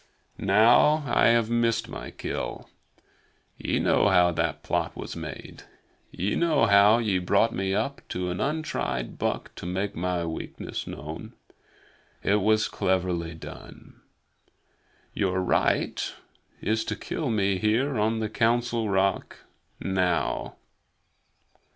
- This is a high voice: No, low, 100 Hz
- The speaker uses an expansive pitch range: No, average, 4.0 semitones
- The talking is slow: Yes, slow, 125 wpm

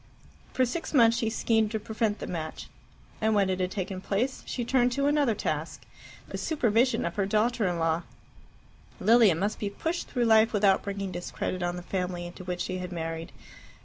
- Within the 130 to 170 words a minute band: No, average, 190 wpm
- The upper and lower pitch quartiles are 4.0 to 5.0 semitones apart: Yes, average, 4.3 semitones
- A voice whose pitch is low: No, high, 205 Hz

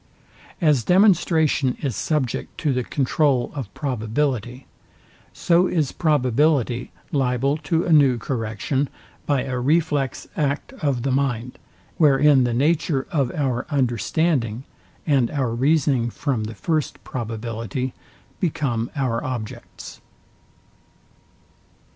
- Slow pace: Yes, slow, 110 wpm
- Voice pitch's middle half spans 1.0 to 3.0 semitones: No, average, 3.7 semitones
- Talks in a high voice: No, low, 135 Hz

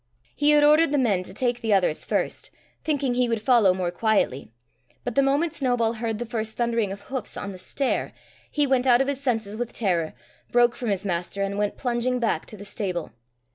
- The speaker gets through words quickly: Yes, fast, 215 wpm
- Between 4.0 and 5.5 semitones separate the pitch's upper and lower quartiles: Yes, average, 4.3 semitones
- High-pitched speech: Yes, high, 235 Hz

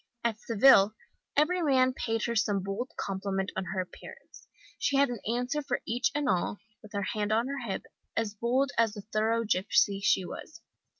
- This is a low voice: No, high, 225 Hz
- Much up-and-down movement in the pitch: No, average, 4.2 semitones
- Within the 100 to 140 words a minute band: No, average, 185 wpm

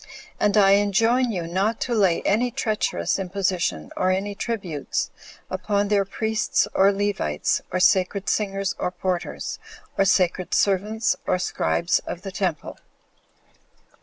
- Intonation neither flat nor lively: No, narrow, 2.3 semitones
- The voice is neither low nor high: No, high, 195 Hz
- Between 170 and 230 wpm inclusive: No, slow, 135 wpm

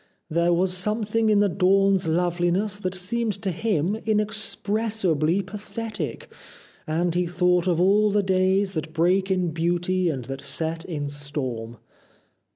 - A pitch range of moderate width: Yes, average, 3.4 semitones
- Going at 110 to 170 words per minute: Yes, average, 140 wpm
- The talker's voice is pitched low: No, medium, 185 Hz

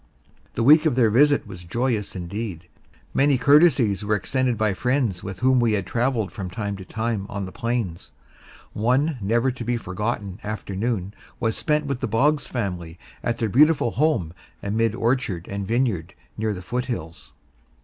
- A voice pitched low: Yes, low, 115 Hz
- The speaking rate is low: No, average, 165 wpm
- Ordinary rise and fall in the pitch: Yes, average, 4.5 semitones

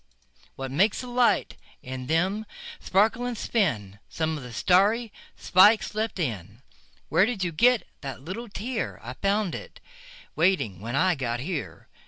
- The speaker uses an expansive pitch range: Yes, wide, 8.5 semitones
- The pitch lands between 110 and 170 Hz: No, medium, 180 Hz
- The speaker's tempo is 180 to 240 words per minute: No, average, 140 wpm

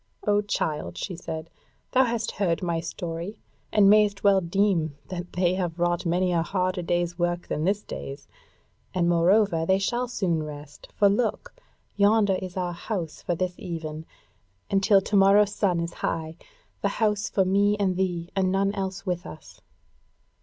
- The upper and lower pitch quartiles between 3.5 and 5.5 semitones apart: No, average, 3.0 semitones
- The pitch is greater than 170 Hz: Yes, medium, 185 Hz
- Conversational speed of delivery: Yes, average, 170 wpm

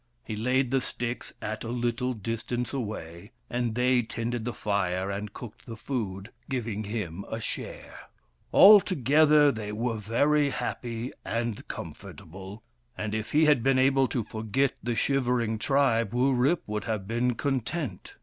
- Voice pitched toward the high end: No, low, 120 Hz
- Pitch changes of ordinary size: Yes, average, 3.4 semitones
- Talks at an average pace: Yes, average, 150 wpm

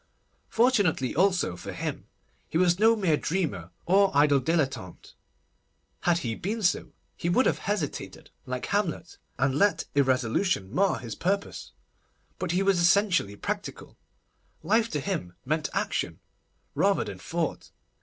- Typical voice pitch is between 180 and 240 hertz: No, medium, 170 Hz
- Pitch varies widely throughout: Yes, wide, 6.7 semitones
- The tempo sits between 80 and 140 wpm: Yes, slow, 135 wpm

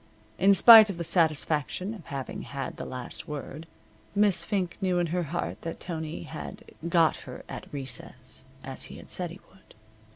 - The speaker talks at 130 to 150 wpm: No, average, 175 wpm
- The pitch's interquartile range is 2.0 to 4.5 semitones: Yes, average, 3.9 semitones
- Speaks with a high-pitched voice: No, medium, 165 Hz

